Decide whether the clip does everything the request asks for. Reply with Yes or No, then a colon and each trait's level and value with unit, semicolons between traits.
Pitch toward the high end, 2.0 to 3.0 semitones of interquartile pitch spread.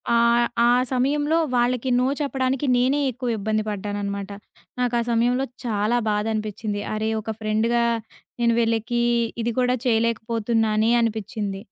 Yes: high, 230 Hz; narrow, 2.5 semitones